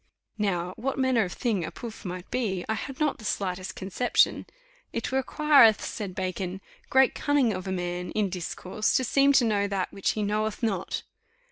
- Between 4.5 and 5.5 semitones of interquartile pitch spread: Yes, average, 5.0 semitones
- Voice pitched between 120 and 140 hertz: No, high, 210 Hz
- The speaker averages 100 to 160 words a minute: No, average, 180 wpm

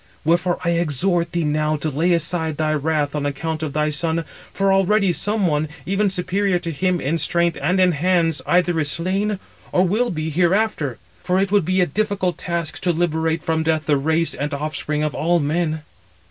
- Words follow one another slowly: No, average, 195 wpm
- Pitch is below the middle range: No, medium, 170 Hz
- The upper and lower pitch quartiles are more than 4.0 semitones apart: No, average, 3.0 semitones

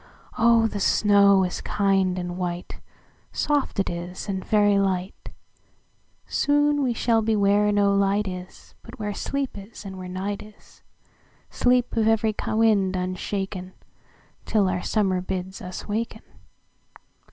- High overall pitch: Yes, high, 200 Hz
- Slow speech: Yes, slow, 120 wpm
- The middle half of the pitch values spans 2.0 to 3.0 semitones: Yes, average, 2.7 semitones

